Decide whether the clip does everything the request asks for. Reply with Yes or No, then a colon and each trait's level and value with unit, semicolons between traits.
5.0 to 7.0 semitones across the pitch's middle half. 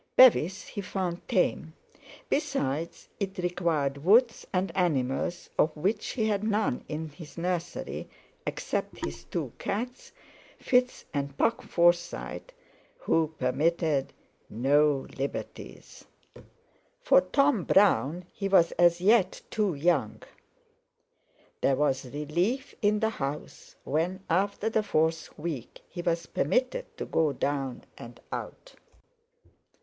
Yes: wide, 5.6 semitones